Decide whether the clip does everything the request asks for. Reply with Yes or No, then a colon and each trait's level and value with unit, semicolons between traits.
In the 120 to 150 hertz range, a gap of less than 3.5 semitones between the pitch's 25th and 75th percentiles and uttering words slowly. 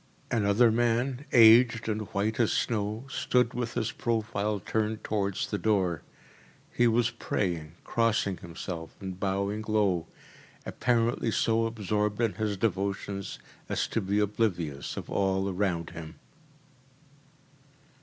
No: low, 105 Hz; average, 2.8 semitones; slow, 125 wpm